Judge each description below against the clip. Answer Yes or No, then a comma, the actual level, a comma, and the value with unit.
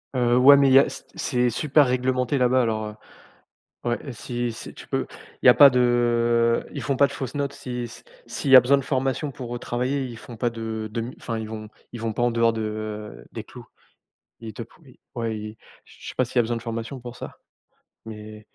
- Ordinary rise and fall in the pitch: No, narrow, 2.3 semitones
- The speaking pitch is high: No, low, 120 Hz